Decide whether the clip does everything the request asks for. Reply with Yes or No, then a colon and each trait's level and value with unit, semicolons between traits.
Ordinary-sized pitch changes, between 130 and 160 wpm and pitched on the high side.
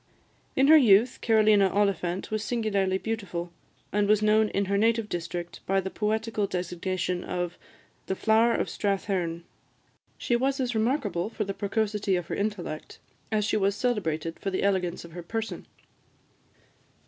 Yes: average, 3.3 semitones; average, 155 wpm; high, 200 Hz